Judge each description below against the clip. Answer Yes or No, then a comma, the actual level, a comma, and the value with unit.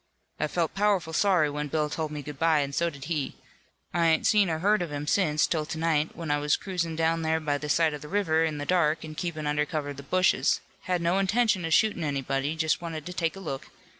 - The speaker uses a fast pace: Yes, fast, 255 wpm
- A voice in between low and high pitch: Yes, medium, 160 Hz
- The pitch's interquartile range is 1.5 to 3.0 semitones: Yes, average, 2.7 semitones